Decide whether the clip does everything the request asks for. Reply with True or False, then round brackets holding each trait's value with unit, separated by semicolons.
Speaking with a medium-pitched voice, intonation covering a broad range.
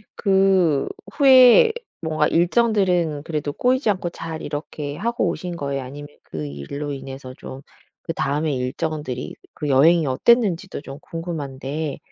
False (155 Hz; 4.8 semitones)